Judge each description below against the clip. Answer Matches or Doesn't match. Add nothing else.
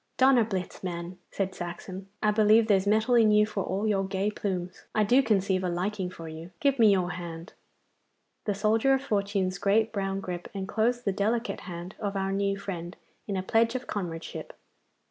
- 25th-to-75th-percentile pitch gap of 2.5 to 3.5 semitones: Matches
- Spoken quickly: Doesn't match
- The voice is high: Matches